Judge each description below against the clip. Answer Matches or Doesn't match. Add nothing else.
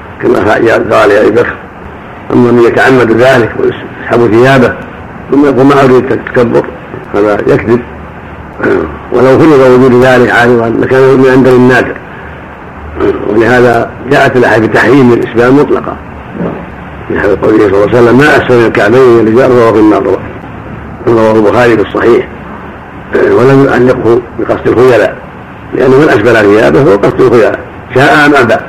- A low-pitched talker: Matches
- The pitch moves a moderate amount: Doesn't match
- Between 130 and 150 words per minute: Matches